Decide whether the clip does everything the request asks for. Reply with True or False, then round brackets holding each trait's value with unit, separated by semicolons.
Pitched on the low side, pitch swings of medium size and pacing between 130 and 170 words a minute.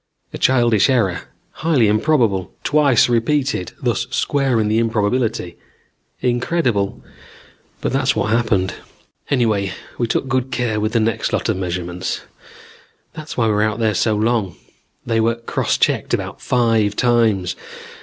True (115 Hz; 3.0 semitones; 140 wpm)